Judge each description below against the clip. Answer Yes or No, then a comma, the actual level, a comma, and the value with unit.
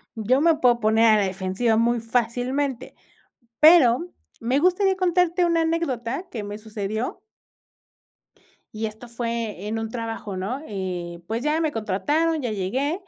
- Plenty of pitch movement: Yes, wide, 5.9 semitones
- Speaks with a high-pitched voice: Yes, high, 235 Hz